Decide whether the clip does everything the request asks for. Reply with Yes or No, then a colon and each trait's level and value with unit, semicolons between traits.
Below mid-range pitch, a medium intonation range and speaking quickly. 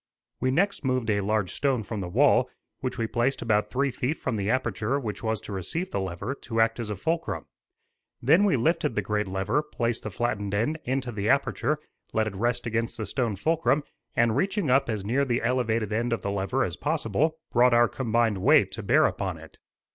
Yes: low, 120 Hz; average, 4.2 semitones; fast, 210 wpm